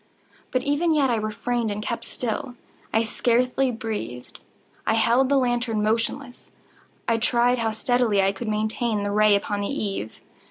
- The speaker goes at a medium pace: Yes, average, 160 wpm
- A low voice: No, high, 230 Hz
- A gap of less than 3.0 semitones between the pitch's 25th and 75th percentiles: Yes, narrow, 2.6 semitones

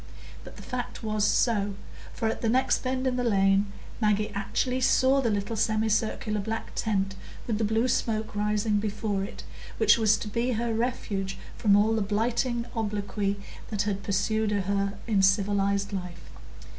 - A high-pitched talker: Yes, high, 210 Hz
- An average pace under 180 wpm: Yes, average, 165 wpm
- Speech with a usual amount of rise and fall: No, narrow, 2.2 semitones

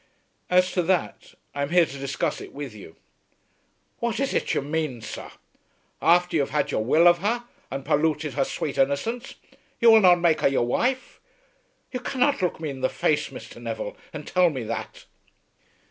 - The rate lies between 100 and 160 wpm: No, average, 190 wpm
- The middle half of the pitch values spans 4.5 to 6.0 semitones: Yes, wide, 5.4 semitones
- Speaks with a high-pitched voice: No, medium, 160 Hz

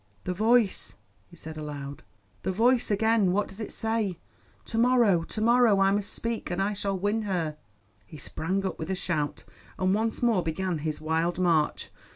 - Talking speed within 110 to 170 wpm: No, average, 185 wpm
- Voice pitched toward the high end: Yes, high, 195 Hz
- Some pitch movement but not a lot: Yes, average, 4.9 semitones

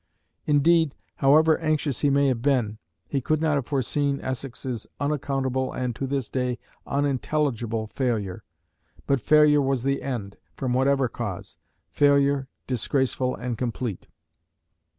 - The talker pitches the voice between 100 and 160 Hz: Yes, low, 135 Hz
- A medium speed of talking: No, slow, 130 wpm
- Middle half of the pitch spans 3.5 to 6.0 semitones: No, narrow, 2.6 semitones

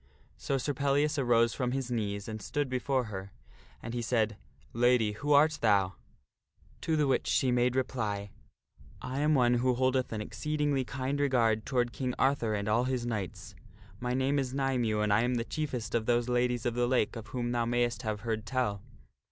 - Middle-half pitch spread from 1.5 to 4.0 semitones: Yes, average, 2.9 semitones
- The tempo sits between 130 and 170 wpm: No, average, 200 wpm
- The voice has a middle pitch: No, low, 120 Hz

